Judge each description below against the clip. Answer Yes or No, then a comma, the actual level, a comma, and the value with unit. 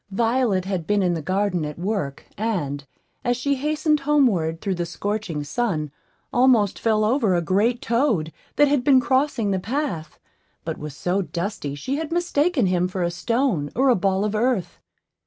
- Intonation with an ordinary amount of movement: No, wide, 6.6 semitones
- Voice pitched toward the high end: Yes, high, 205 Hz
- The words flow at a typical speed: Yes, average, 175 wpm